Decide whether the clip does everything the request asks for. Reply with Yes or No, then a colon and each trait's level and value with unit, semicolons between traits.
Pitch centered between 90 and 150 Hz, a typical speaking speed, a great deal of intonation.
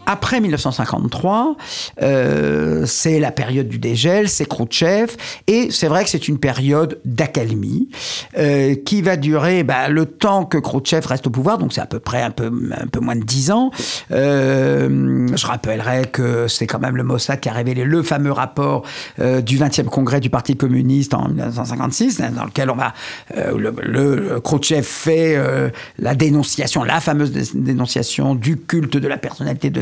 No: low, 135 Hz; average, 175 wpm; average, 4.1 semitones